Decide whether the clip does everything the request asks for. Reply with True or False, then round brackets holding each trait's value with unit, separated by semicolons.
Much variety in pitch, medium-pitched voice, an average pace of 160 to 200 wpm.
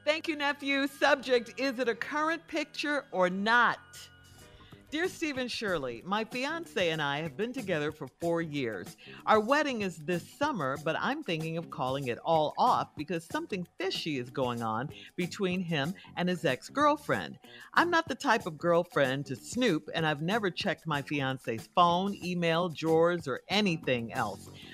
True (8.9 semitones; 175 Hz; 165 wpm)